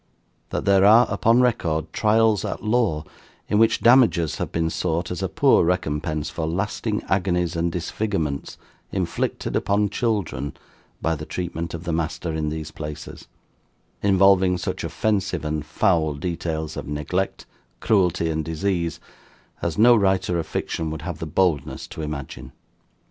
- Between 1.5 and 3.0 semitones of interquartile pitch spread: No, average, 4.0 semitones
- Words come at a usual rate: Yes, average, 150 wpm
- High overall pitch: No, very low, 85 Hz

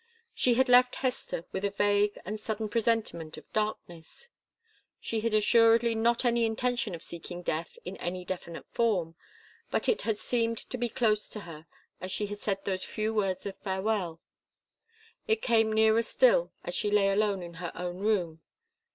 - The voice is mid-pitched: No, high, 210 Hz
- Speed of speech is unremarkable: Yes, average, 175 wpm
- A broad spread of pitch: No, average, 3.8 semitones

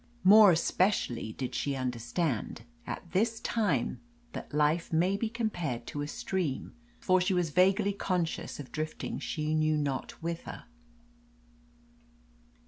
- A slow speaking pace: Yes, slow, 130 wpm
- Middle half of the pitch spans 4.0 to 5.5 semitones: Yes, average, 4.7 semitones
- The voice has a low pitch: No, medium, 170 Hz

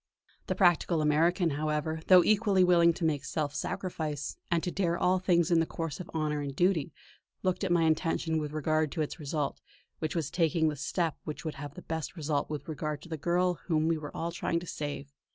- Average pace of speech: No, fast, 215 wpm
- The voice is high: No, medium, 160 Hz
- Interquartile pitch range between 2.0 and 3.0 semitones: Yes, narrow, 2.4 semitones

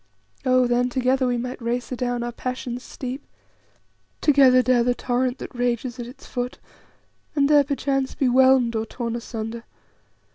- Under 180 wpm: Yes, average, 155 wpm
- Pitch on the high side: Yes, very high, 250 Hz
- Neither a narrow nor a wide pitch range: No, narrow, 1.3 semitones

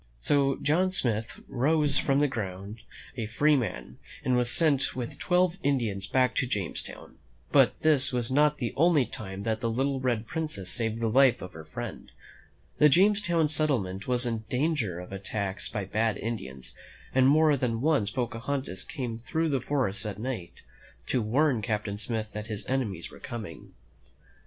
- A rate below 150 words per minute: No, average, 170 wpm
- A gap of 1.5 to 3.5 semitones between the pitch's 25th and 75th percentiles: No, average, 5.1 semitones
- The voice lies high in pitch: No, low, 120 Hz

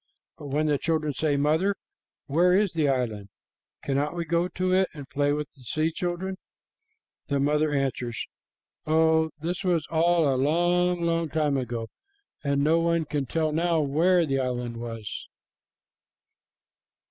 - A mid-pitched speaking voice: Yes, medium, 155 Hz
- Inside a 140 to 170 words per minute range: Yes, average, 150 wpm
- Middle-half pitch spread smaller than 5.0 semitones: Yes, average, 3.3 semitones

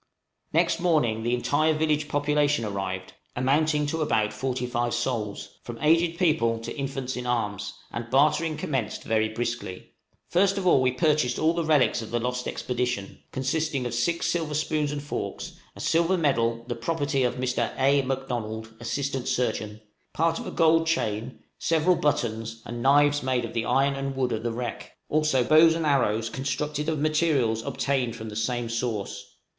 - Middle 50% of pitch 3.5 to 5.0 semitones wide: Yes, average, 4.6 semitones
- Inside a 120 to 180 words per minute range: Yes, average, 170 wpm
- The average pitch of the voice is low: Yes, low, 130 Hz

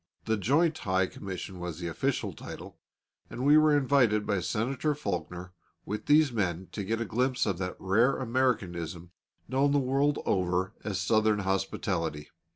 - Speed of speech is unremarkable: Yes, average, 160 wpm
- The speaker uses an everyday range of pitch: No, wide, 6.2 semitones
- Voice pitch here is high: No, low, 105 Hz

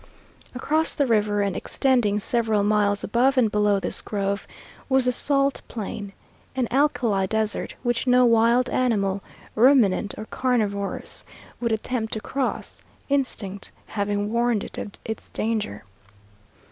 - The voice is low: No, high, 220 Hz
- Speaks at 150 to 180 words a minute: No, slow, 135 wpm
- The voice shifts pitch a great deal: No, average, 3.5 semitones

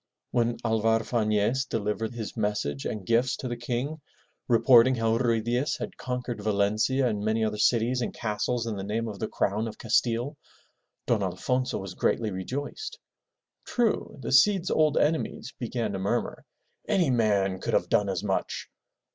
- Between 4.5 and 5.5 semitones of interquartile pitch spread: No, average, 3.1 semitones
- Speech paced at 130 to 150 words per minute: No, average, 165 wpm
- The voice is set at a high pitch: No, low, 115 Hz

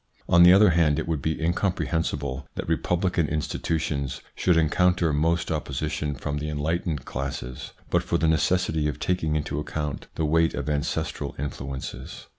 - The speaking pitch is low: Yes, very low, 75 Hz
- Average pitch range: No, narrow, 2.3 semitones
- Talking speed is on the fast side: No, average, 160 wpm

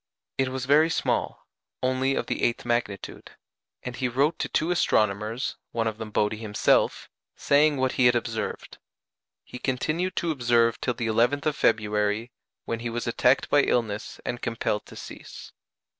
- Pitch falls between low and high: No, low, 120 Hz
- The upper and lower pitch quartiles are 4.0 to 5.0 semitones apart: No, average, 3.1 semitones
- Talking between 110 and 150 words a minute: No, average, 165 wpm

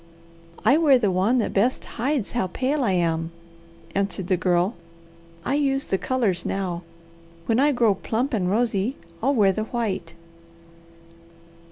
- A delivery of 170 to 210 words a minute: No, average, 150 wpm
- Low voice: No, high, 215 Hz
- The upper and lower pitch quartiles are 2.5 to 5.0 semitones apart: No, wide, 5.4 semitones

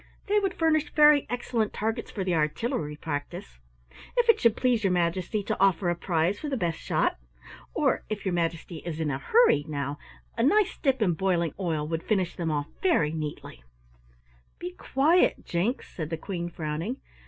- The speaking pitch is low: No, medium, 180 Hz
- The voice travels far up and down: Yes, wide, 7.3 semitones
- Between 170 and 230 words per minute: Yes, average, 180 wpm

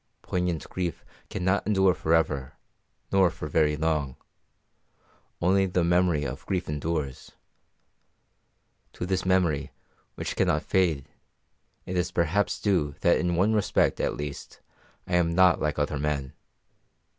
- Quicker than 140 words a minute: No, slow, 135 wpm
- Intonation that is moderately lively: Yes, average, 3.6 semitones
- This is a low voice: Yes, very low, 85 Hz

